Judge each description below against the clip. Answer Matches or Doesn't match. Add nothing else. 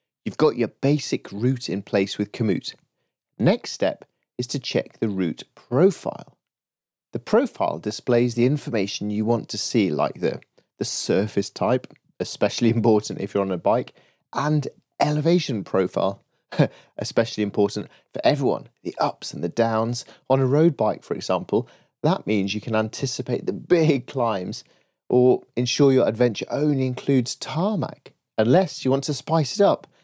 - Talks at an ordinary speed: Matches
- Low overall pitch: Matches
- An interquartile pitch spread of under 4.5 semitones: Doesn't match